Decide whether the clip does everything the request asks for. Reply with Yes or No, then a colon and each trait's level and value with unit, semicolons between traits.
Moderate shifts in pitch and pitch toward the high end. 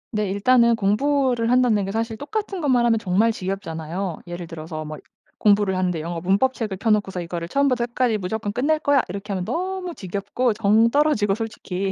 Yes: average, 4.9 semitones; high, 210 Hz